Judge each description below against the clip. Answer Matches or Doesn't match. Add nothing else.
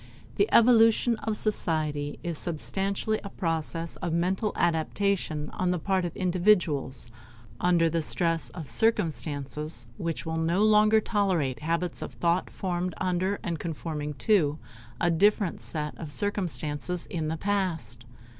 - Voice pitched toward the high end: Doesn't match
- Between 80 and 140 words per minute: Matches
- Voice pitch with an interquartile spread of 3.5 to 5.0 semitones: Matches